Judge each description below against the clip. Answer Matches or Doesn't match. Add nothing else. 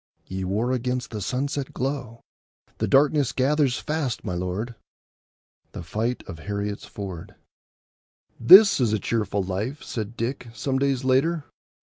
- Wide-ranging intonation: Doesn't match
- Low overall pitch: Matches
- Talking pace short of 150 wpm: Matches